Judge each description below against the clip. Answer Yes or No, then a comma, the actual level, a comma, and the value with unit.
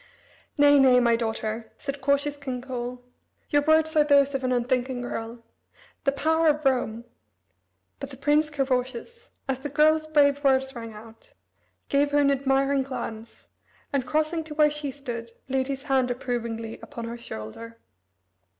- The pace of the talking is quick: No, average, 160 wpm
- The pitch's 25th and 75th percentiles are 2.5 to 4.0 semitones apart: Yes, average, 3.1 semitones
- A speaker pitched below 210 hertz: No, very high, 270 Hz